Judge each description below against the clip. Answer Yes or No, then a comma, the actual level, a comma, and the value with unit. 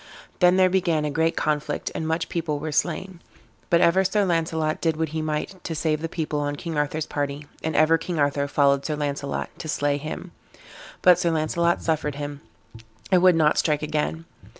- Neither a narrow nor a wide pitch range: No, narrow, 2.3 semitones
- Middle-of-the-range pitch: Yes, medium, 155 Hz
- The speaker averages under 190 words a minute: No, average, 195 wpm